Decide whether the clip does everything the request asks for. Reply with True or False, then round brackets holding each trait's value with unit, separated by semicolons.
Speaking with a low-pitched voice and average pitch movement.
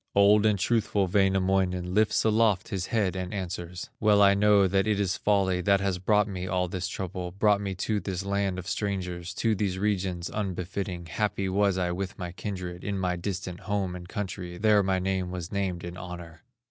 False (95 Hz; 2.0 semitones)